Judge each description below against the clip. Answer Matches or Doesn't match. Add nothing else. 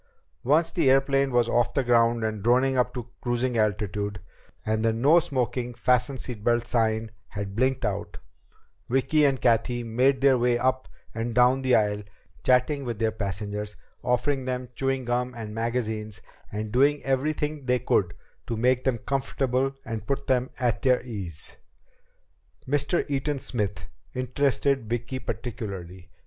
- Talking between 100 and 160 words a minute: Matches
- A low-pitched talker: Matches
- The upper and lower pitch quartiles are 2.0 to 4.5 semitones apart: Matches